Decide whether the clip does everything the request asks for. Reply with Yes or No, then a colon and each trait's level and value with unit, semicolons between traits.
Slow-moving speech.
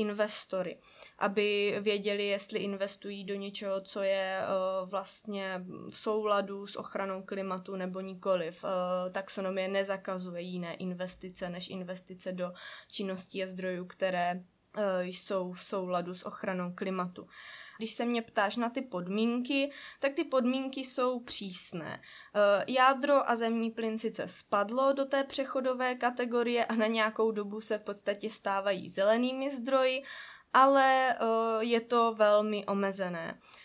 No: average, 125 wpm